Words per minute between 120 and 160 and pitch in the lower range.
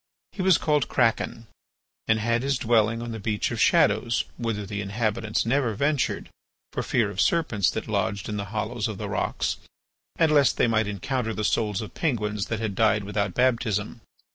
No: average, 185 wpm; low, 110 Hz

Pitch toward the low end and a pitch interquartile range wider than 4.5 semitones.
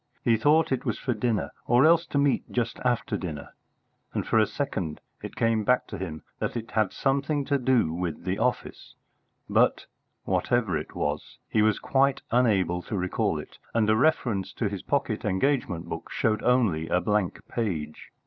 Yes: low, 110 Hz; average, 5.3 semitones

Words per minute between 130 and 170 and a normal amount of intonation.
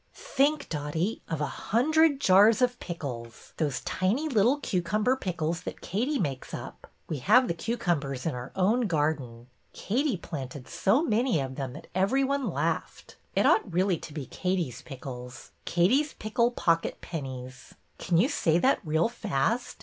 No: average, 155 wpm; wide, 8.7 semitones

